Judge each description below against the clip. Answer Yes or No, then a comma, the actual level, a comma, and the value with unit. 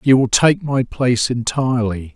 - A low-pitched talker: Yes, low, 125 Hz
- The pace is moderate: Yes, average, 165 wpm